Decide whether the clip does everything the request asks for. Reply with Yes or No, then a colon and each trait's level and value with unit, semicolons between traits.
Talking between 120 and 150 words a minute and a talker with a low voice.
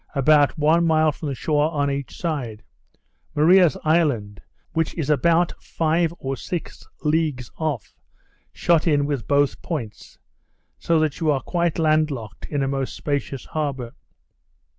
No: average, 145 wpm; medium, 150 Hz